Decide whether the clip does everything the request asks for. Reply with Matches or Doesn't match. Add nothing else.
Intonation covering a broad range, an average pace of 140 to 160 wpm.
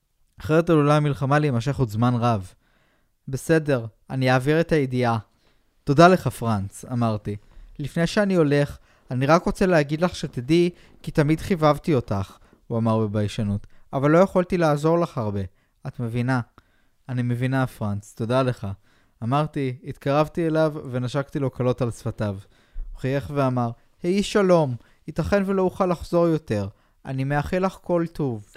Matches